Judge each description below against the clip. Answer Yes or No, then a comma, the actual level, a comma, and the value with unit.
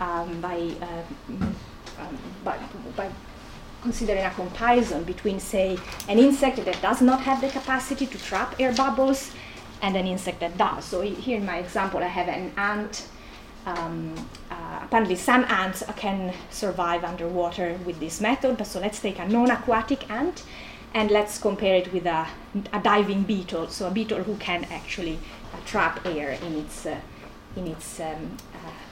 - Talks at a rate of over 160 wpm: Yes, average, 170 wpm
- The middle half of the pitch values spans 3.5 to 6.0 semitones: Yes, average, 4.3 semitones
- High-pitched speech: Yes, high, 195 Hz